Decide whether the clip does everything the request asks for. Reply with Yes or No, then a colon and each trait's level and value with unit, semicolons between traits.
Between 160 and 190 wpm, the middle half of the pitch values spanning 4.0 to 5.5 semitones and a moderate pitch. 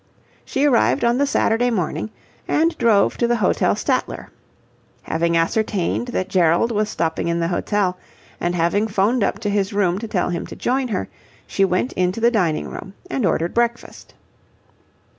No: average, 170 wpm; average, 5.2 semitones; high, 200 Hz